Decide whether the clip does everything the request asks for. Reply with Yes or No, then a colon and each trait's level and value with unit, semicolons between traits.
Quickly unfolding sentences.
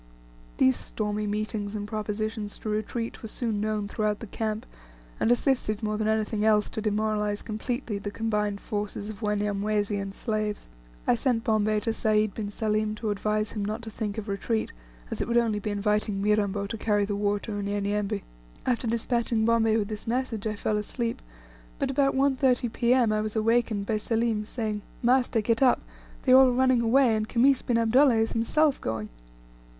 No: average, 185 wpm